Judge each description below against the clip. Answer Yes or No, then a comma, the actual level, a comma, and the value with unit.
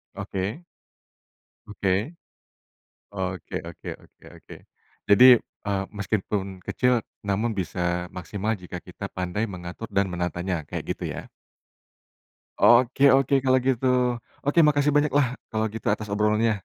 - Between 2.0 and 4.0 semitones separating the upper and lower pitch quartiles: No, average, 5.1 semitones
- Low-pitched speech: Yes, low, 105 Hz